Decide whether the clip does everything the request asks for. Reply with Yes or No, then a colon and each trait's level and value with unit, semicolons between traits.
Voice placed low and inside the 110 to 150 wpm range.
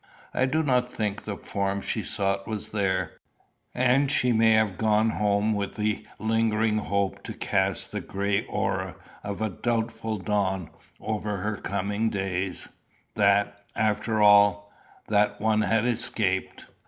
Yes: low, 105 Hz; average, 140 wpm